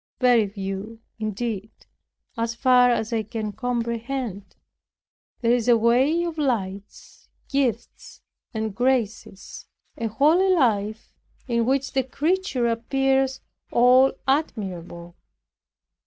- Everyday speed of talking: No, slow, 105 wpm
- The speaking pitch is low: No, high, 235 Hz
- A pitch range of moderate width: Yes, average, 3.6 semitones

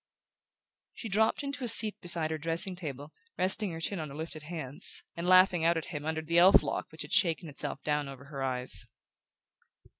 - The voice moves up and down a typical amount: Yes, average, 3.8 semitones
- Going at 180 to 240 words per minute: Yes, average, 200 wpm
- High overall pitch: No, medium, 165 Hz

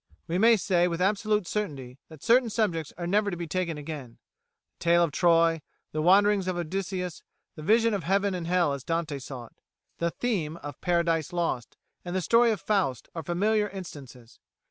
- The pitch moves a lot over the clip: No, average, 4.0 semitones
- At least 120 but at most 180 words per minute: No, average, 190 wpm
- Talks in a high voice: No, medium, 175 Hz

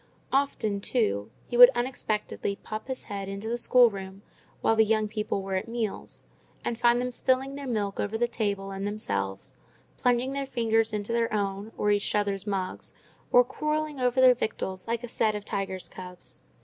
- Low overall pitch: No, high, 220 Hz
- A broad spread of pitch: No, average, 3.5 semitones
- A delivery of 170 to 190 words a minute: Yes, average, 180 wpm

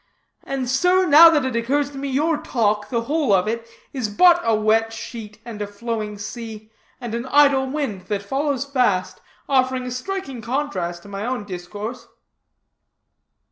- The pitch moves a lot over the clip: No, average, 4.7 semitones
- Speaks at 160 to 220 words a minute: Yes, average, 170 wpm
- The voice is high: Yes, high, 235 Hz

